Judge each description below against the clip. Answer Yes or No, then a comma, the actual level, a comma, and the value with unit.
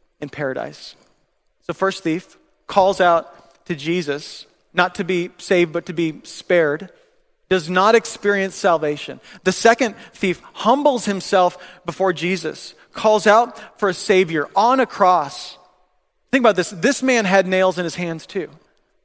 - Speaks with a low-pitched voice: No, medium, 185 Hz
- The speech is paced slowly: No, average, 150 wpm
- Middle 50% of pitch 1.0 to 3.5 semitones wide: No, average, 3.9 semitones